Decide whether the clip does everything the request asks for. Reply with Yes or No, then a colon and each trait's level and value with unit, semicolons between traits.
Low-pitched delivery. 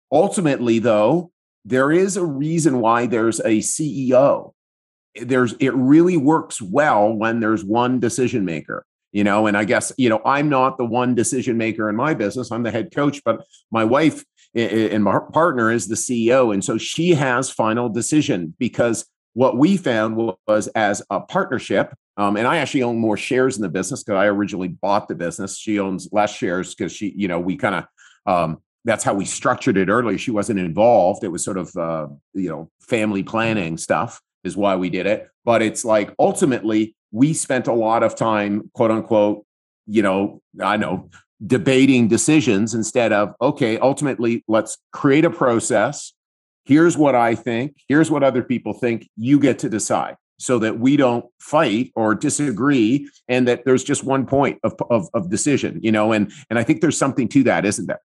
Yes: low, 115 Hz